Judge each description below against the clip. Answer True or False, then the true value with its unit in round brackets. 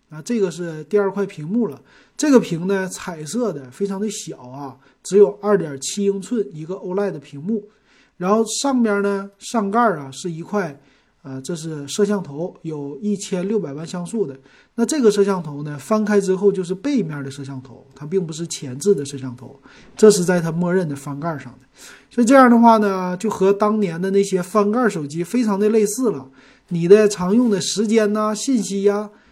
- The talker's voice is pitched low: False (195 Hz)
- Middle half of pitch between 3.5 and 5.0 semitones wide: False (5.6 semitones)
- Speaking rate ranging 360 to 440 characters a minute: False (290 characters per minute)